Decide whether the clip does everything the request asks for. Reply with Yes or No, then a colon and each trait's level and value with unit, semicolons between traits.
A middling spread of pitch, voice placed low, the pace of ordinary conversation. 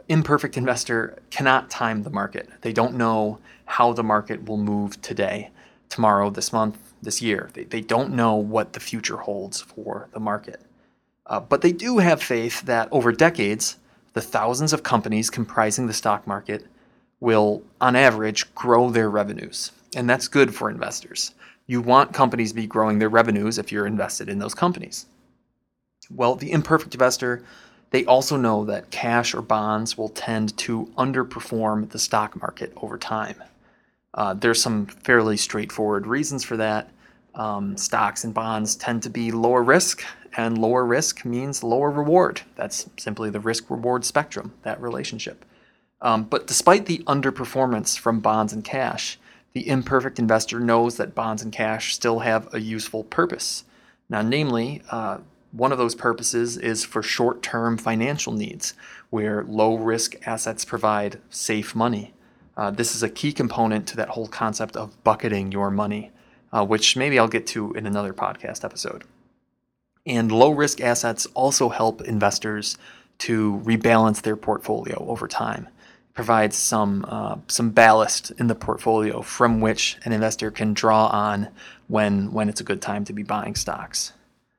No: narrow, 2.1 semitones; low, 115 Hz; average, 160 wpm